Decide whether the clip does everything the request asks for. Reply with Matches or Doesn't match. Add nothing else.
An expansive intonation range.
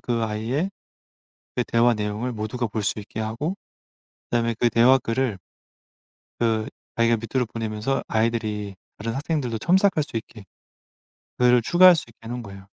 Doesn't match